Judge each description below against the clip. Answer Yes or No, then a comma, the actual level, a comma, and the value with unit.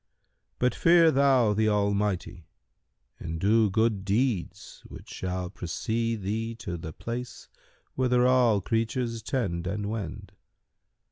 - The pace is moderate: No, slow, 120 wpm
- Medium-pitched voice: No, low, 110 Hz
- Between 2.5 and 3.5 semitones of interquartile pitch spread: No, average, 4.1 semitones